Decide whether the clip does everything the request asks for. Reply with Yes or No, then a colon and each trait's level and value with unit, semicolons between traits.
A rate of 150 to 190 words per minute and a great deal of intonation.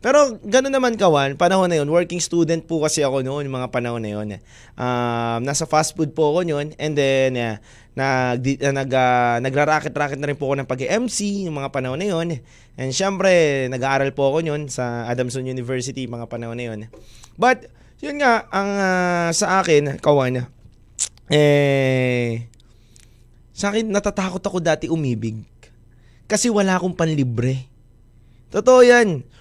Yes: fast, 155 wpm; wide, 6.1 semitones